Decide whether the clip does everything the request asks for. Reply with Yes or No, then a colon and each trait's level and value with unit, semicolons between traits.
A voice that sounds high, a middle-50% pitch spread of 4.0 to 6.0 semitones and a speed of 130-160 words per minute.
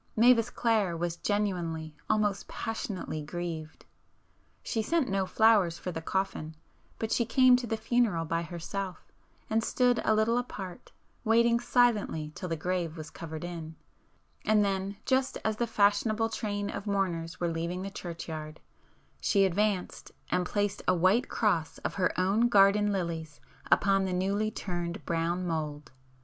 Yes: high, 195 Hz; average, 4.3 semitones; average, 150 wpm